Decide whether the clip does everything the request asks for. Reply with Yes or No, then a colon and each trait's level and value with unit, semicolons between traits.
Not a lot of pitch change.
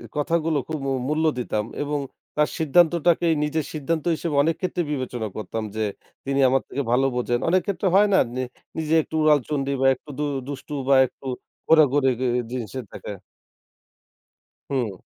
No: average, 3.4 semitones